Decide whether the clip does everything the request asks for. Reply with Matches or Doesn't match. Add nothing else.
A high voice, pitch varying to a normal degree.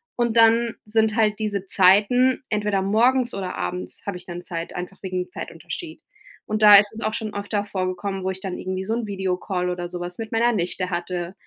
Matches